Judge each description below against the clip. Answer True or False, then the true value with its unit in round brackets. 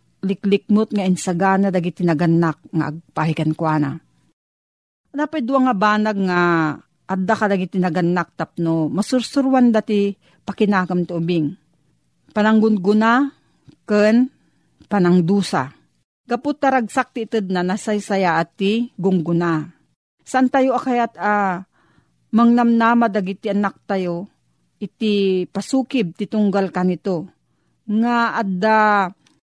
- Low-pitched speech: False (195 Hz)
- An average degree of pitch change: True (4.3 semitones)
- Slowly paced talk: True (100 wpm)